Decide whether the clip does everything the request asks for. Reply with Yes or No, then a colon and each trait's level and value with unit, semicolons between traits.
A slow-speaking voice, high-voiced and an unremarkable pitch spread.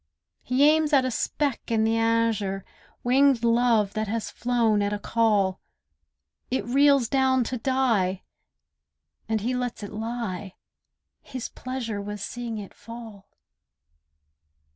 Yes: slow, 130 wpm; high, 230 Hz; average, 3.5 semitones